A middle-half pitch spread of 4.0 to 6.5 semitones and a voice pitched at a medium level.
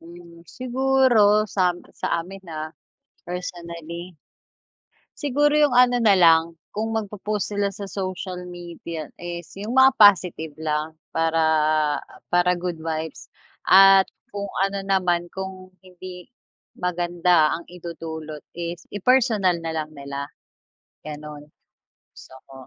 No: average, 3.3 semitones; medium, 180 Hz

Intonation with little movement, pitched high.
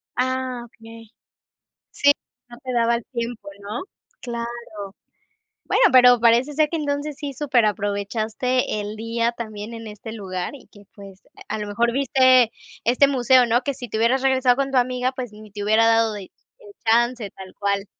No: average, 3.0 semitones; high, 235 Hz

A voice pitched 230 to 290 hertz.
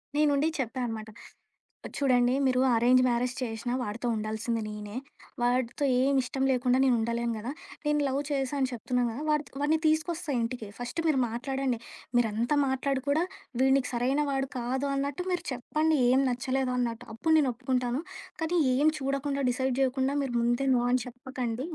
Yes: very high, 255 Hz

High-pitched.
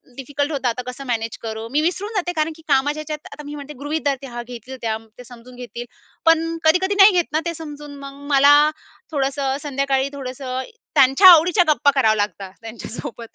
Yes: very high, 280 Hz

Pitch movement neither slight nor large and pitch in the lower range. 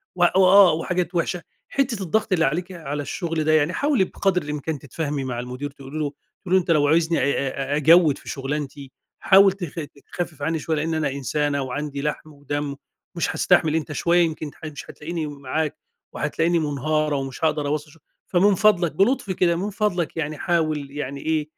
No: average, 3.2 semitones; medium, 155 Hz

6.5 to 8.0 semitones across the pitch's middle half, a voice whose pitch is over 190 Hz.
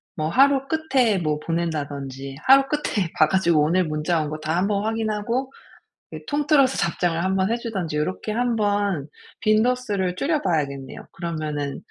No: wide, 6.9 semitones; medium, 185 Hz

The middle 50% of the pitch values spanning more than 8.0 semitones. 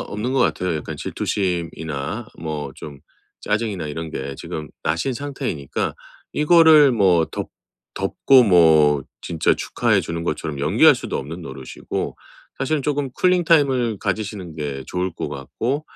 Yes: wide, 8.9 semitones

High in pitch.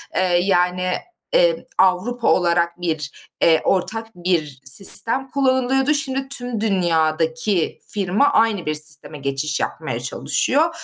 No: medium, 180 Hz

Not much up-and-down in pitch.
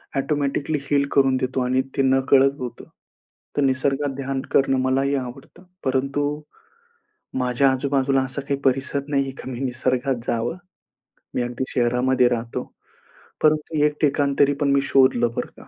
Yes: narrow, 1.4 semitones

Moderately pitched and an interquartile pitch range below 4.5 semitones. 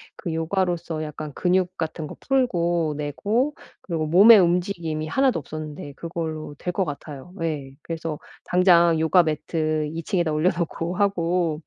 Yes: medium, 165 Hz; narrow, 2.6 semitones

